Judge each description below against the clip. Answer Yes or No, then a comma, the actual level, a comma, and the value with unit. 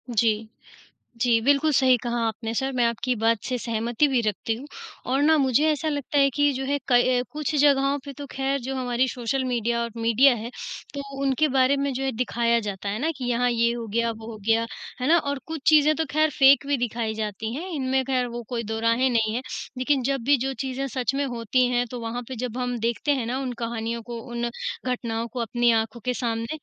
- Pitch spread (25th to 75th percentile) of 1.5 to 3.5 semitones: Yes, average, 2.9 semitones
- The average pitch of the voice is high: Yes, high, 245 Hz